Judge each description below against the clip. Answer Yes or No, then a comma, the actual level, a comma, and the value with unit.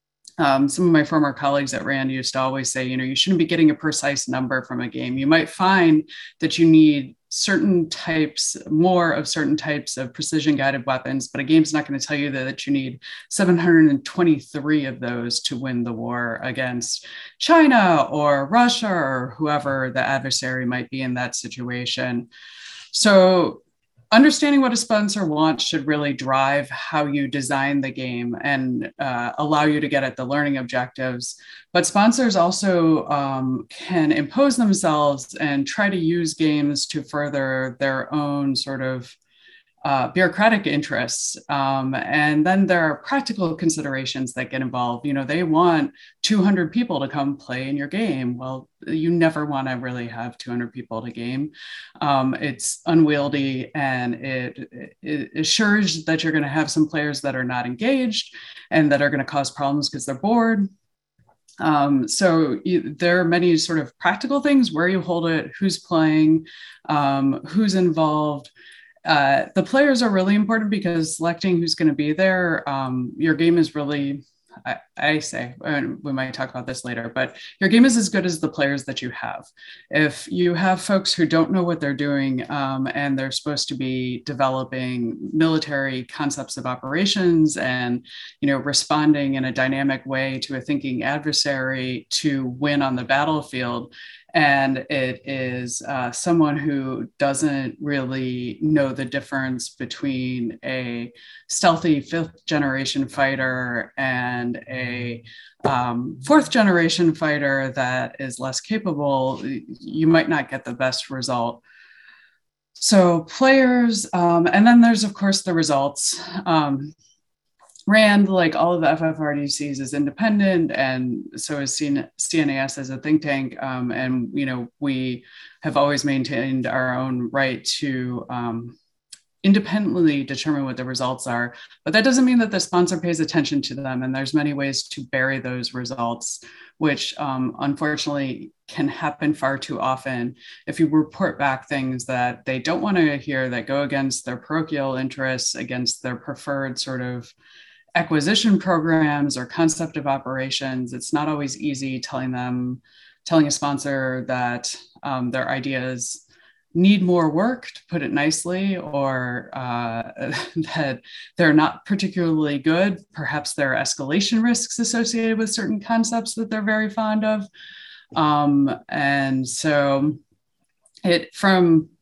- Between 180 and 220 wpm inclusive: No, average, 160 wpm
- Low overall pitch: No, medium, 145 Hz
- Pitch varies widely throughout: No, average, 4.3 semitones